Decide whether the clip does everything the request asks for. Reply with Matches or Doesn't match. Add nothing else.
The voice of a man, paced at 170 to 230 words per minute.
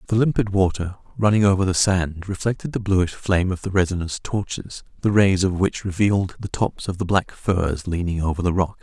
Matches